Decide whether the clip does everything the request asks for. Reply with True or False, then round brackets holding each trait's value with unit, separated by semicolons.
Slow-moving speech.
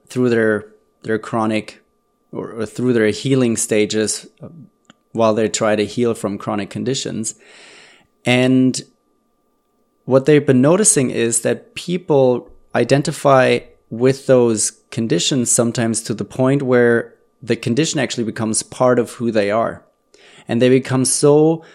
True (130 wpm)